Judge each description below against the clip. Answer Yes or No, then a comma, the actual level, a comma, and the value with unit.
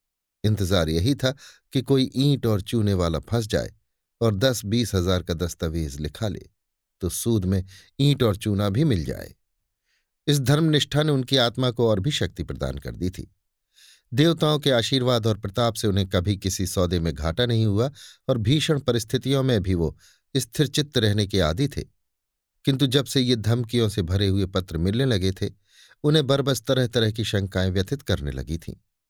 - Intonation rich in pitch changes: Yes, wide, 5.9 semitones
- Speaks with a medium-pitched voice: No, low, 110 Hz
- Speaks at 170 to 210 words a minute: Yes, average, 185 wpm